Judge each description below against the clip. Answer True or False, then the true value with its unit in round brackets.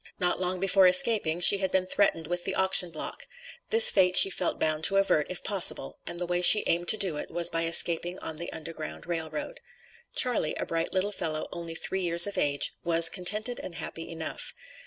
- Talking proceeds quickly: True (210 wpm)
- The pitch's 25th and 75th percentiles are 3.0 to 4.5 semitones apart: False (2.6 semitones)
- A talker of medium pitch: True (175 Hz)